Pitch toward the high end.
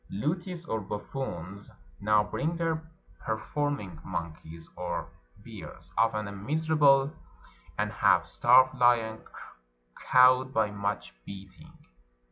No: low, 115 Hz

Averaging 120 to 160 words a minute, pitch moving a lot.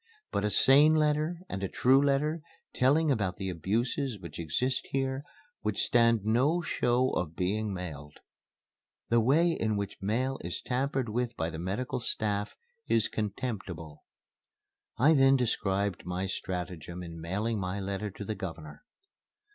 Yes: average, 145 wpm; wide, 6.0 semitones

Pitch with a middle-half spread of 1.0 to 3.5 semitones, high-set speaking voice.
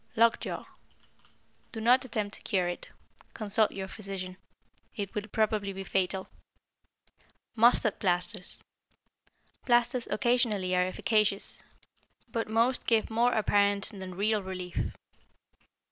Yes: average, 3.0 semitones; high, 205 Hz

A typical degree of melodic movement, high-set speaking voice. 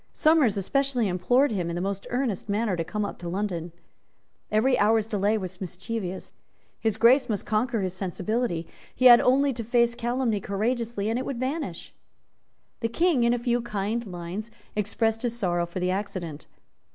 Yes: average, 4.1 semitones; high, 215 Hz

